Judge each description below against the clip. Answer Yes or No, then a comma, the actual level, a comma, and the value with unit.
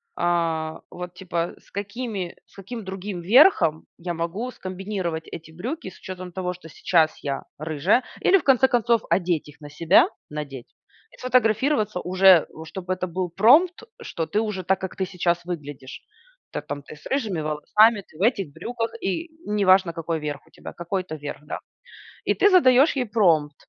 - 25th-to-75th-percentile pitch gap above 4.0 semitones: Yes, average, 4.7 semitones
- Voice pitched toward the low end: No, medium, 185 Hz